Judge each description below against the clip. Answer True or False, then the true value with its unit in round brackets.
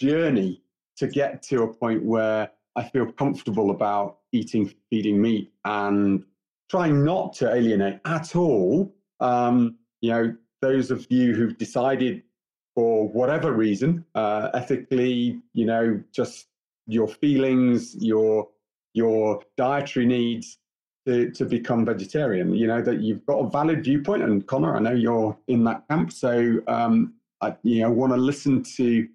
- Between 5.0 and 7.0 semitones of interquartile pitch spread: False (3.3 semitones)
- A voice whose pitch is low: True (115 Hz)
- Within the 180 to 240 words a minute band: False (150 wpm)